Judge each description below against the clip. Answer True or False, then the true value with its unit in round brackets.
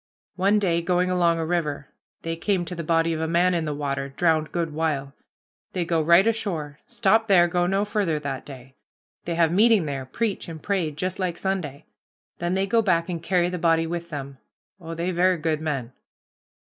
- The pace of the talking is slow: False (200 wpm)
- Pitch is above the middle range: False (170 Hz)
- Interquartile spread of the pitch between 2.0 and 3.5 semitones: True (2.8 semitones)